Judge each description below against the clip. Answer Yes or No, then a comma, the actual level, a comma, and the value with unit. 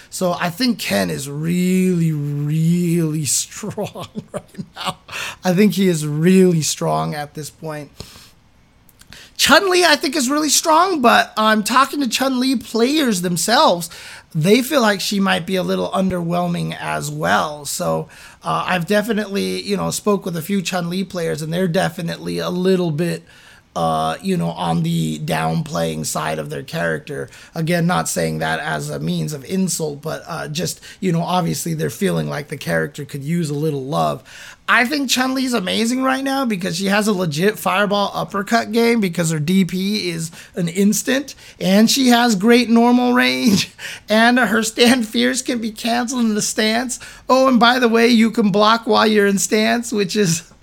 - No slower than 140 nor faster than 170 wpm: No, average, 180 wpm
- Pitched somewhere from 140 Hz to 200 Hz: Yes, high, 190 Hz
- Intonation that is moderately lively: No, wide, 6.2 semitones